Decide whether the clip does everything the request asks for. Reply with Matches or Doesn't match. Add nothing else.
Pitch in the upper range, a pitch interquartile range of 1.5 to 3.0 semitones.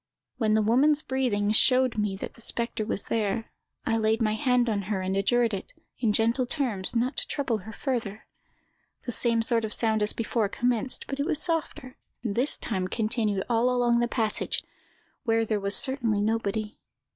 Matches